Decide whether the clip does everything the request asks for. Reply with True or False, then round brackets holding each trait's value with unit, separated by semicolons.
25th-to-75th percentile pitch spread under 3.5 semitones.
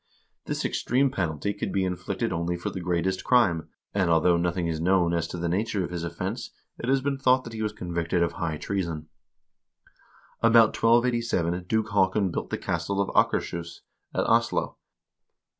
False (4.3 semitones)